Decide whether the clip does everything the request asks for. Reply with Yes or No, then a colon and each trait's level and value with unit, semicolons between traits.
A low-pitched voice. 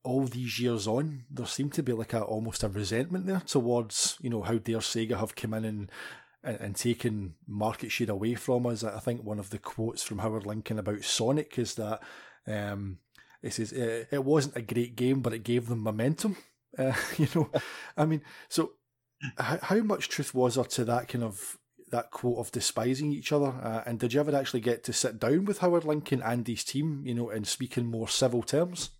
Yes: low, 120 Hz